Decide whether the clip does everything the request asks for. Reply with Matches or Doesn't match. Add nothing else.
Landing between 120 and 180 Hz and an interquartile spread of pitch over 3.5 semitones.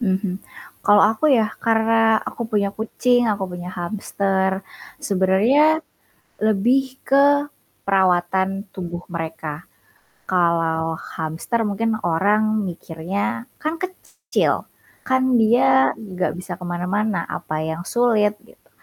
Doesn't match